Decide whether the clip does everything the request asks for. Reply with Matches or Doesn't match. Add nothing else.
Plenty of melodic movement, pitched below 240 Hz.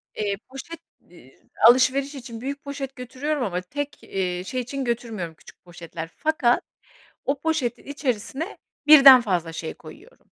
Doesn't match